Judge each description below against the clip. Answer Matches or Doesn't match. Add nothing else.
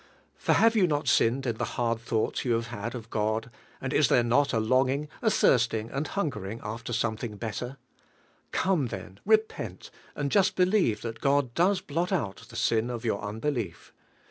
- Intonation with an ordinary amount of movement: Matches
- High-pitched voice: Doesn't match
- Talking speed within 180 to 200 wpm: Matches